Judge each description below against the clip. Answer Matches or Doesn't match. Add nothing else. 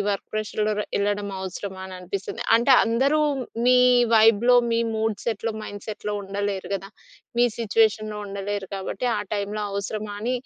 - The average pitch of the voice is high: Matches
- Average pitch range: Doesn't match